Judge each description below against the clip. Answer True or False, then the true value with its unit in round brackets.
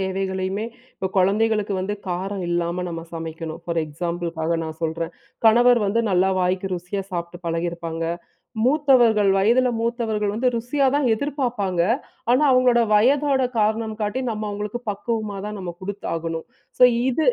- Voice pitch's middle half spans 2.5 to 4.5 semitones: False (5.1 semitones)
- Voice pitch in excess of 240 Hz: False (200 Hz)